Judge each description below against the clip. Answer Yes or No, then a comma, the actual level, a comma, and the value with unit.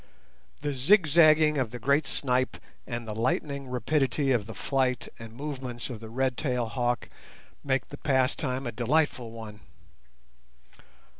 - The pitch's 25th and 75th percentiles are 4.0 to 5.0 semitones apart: No, average, 3.2 semitones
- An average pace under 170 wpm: Yes, average, 140 wpm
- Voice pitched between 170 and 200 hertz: No, low, 130 Hz